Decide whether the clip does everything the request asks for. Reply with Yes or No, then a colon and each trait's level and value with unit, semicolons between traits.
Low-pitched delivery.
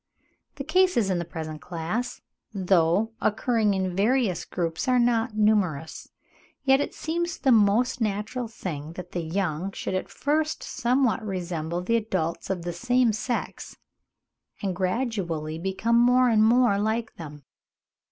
No: high, 210 Hz